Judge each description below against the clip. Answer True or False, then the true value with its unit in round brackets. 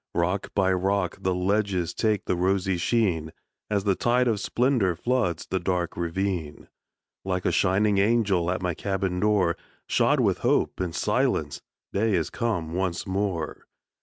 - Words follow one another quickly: False (155 wpm)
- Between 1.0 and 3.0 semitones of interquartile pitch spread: True (2.6 semitones)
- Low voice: True (95 Hz)